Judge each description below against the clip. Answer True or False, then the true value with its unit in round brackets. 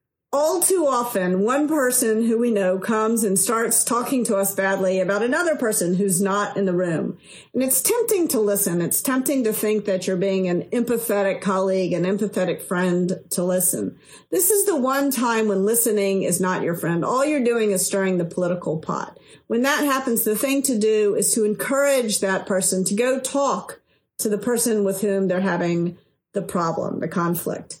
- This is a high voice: True (205 Hz)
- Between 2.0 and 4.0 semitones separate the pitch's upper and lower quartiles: False (4.4 semitones)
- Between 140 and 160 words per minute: False (190 wpm)